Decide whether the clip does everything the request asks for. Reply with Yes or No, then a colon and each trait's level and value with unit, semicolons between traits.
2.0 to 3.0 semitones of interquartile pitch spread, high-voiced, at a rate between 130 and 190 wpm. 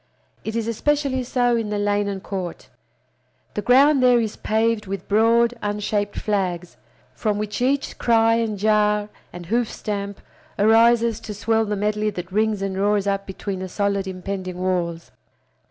Yes: narrow, 2.5 semitones; high, 210 Hz; average, 160 wpm